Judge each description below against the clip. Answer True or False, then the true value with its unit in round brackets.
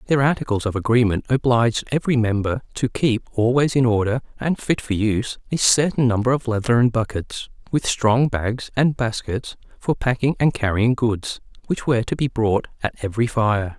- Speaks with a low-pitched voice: True (120 Hz)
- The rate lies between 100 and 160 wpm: False (175 wpm)